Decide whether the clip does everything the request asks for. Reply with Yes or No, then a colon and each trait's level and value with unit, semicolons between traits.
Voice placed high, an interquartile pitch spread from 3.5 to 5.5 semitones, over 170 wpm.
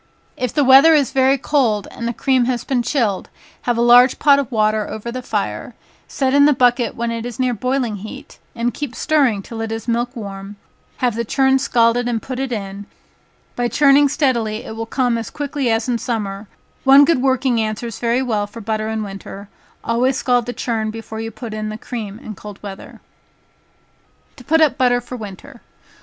No: high, 240 Hz; average, 3.1 semitones; average, 200 wpm